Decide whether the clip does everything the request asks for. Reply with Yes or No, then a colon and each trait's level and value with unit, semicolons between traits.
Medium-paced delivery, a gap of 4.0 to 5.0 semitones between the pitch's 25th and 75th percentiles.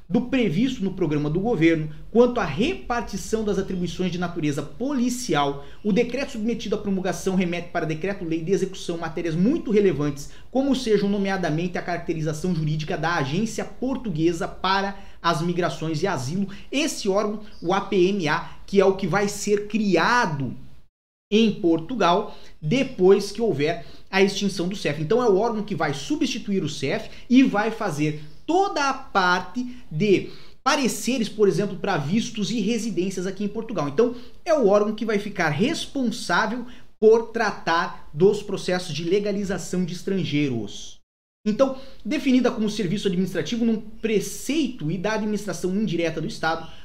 Yes: average, 150 wpm; average, 4.5 semitones